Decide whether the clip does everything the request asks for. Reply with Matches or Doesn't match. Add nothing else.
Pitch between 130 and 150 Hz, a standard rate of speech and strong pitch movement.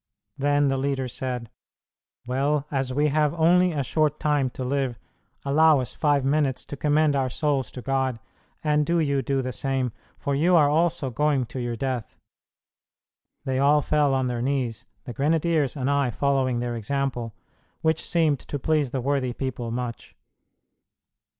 Doesn't match